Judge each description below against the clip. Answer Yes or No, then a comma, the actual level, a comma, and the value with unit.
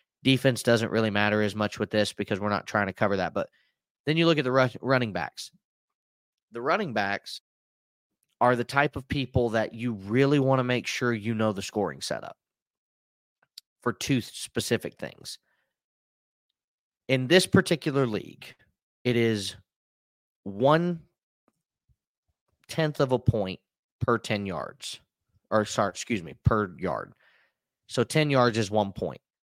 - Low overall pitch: Yes, low, 115 Hz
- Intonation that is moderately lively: Yes, average, 4.2 semitones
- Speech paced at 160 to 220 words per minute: No, average, 150 wpm